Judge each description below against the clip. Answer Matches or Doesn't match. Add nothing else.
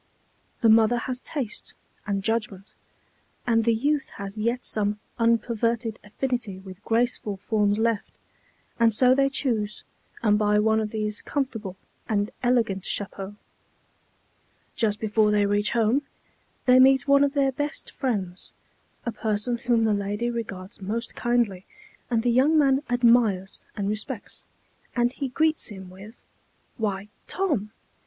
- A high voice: Matches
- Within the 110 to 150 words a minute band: Matches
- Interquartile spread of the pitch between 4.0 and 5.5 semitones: Doesn't match